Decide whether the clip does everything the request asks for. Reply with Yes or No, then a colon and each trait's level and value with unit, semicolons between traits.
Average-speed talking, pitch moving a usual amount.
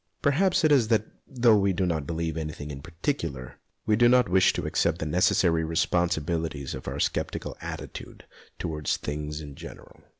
No: average, 175 wpm; wide, 5.9 semitones